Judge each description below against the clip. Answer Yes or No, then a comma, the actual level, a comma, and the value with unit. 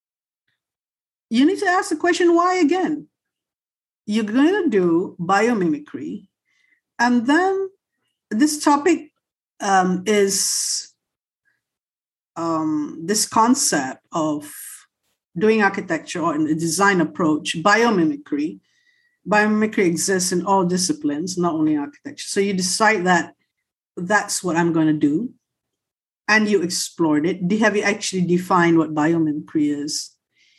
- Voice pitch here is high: Yes, high, 205 Hz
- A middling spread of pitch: No, wide, 9.0 semitones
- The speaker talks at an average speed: No, slow, 120 wpm